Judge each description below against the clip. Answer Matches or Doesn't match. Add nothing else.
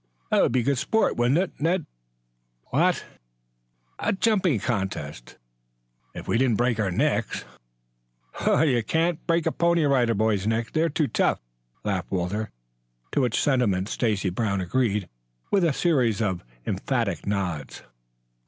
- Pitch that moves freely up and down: Matches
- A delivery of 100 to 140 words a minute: Matches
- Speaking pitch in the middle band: Doesn't match